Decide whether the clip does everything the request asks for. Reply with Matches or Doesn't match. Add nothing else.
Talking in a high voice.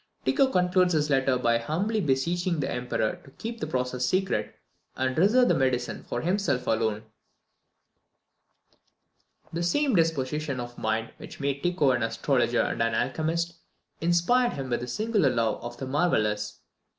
Doesn't match